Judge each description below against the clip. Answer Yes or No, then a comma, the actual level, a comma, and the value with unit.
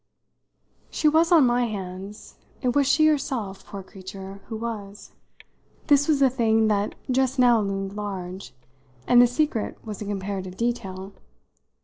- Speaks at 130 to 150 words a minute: Yes, average, 145 wpm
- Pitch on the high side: Yes, high, 220 Hz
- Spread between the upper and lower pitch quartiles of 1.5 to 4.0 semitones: No, average, 4.6 semitones